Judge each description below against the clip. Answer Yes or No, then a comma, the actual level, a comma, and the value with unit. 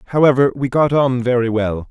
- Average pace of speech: Yes, average, 190 wpm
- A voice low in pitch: Yes, low, 125 Hz